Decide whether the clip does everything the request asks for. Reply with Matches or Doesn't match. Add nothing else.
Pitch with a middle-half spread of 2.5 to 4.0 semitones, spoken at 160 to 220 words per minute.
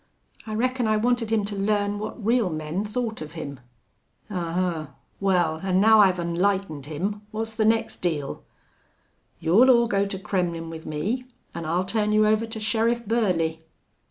Doesn't match